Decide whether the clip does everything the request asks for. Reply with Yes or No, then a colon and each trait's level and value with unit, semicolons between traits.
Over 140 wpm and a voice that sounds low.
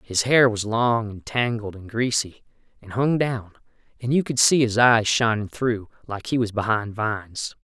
Yes: average, 190 wpm; low, 115 Hz